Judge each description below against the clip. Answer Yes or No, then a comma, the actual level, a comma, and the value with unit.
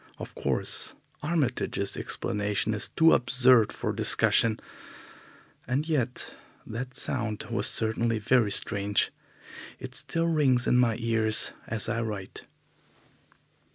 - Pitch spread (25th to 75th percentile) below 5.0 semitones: Yes, average, 3.0 semitones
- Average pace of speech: No, slow, 115 wpm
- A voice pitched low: Yes, low, 115 Hz